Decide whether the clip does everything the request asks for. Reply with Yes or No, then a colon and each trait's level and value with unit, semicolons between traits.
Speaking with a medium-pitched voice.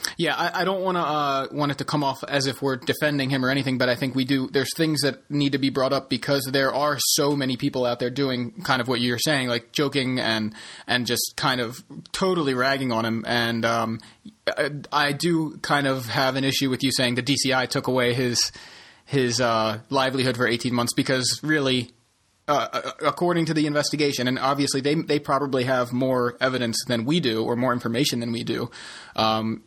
No: low, 130 Hz